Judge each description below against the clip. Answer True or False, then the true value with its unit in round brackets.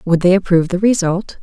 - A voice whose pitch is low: False (185 Hz)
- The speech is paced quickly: True (210 wpm)